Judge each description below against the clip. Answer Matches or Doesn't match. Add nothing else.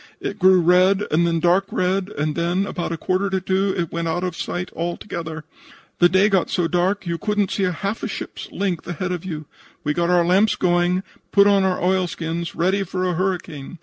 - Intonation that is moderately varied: Doesn't match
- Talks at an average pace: Doesn't match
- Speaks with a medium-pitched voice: Matches